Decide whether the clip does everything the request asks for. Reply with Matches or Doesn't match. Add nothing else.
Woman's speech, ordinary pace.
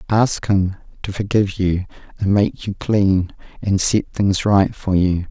Doesn't match